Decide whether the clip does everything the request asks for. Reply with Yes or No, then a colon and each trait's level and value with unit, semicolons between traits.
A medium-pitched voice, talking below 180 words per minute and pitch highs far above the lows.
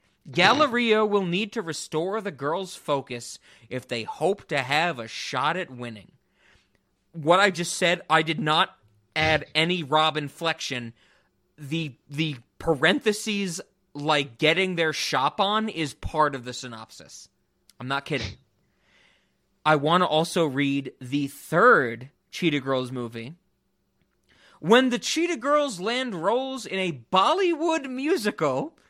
Yes: medium, 160 Hz; slow, 135 wpm; wide, 6.4 semitones